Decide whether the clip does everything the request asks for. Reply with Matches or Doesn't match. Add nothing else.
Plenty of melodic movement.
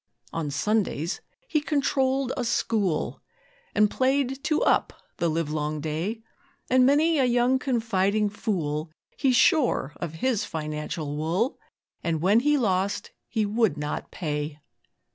Matches